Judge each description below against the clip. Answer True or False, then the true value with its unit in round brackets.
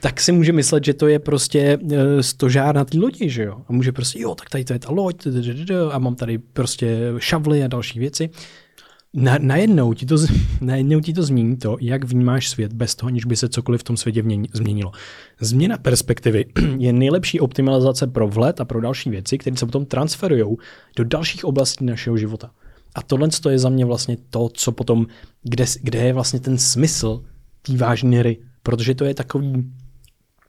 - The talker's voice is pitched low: True (130 Hz)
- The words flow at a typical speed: False (195 wpm)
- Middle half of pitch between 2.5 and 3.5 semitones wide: True (2.9 semitones)